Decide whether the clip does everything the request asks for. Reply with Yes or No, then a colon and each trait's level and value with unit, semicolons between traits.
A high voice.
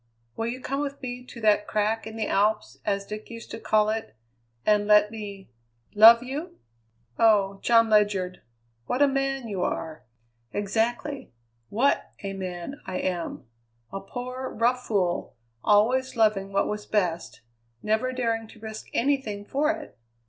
Yes: high, 220 Hz